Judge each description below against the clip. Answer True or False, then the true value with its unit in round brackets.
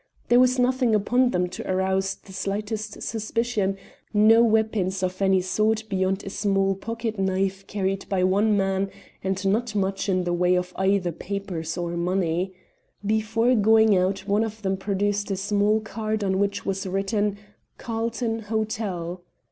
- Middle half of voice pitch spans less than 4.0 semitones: True (2.4 semitones)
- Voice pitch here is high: True (200 Hz)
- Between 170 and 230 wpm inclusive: False (155 wpm)